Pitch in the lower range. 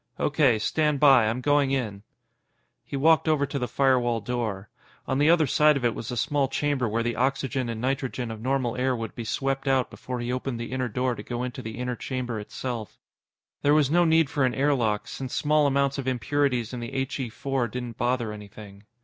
Yes: low, 130 Hz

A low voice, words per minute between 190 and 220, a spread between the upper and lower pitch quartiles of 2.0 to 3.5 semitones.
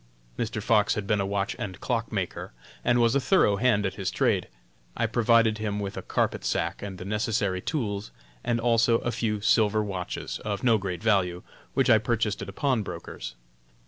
Yes: low, 105 Hz; average, 195 wpm; average, 2.8 semitones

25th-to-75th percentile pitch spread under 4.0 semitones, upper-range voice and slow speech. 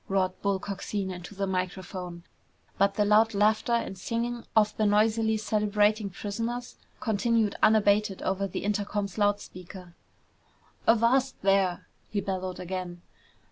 Yes: narrow, 2.4 semitones; high, 205 Hz; slow, 130 wpm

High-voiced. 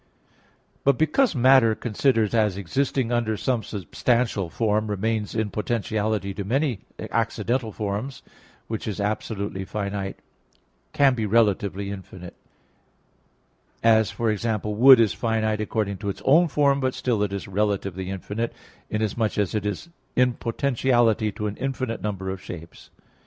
No: low, 110 Hz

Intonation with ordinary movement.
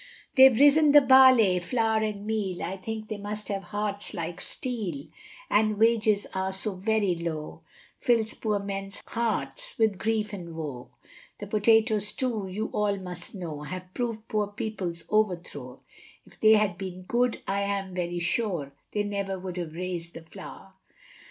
Yes: average, 3.2 semitones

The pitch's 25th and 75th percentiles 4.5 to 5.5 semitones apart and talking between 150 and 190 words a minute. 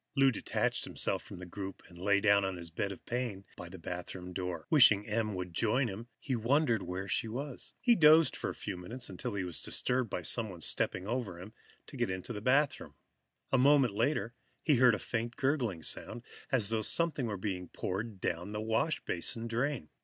No: average, 5.2 semitones; average, 200 wpm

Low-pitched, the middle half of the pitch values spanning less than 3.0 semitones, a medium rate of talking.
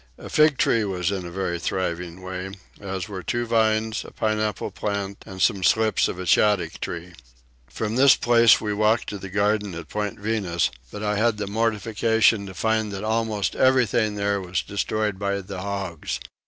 Yes: low, 105 Hz; narrow, 2.5 semitones; average, 175 wpm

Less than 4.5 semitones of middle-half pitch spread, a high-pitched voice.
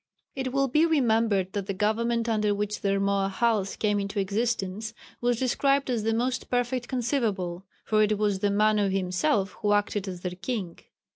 Yes: average, 3.3 semitones; high, 210 Hz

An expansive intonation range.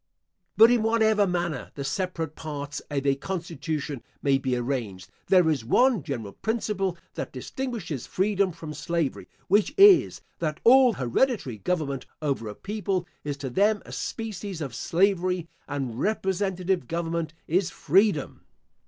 Yes: wide, 6.1 semitones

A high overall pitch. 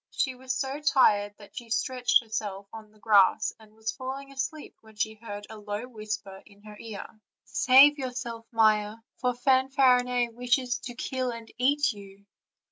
Yes: high, 230 Hz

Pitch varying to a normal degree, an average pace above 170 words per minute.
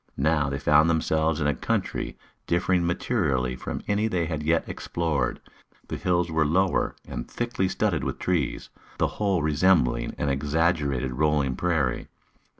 No: average, 3.7 semitones; average, 150 wpm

